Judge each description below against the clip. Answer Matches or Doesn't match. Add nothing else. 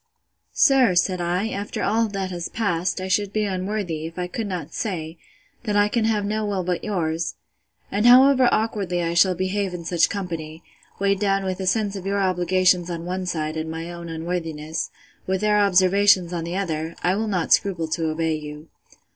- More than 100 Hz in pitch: Matches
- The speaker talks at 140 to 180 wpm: Doesn't match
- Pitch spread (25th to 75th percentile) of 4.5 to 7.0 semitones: Doesn't match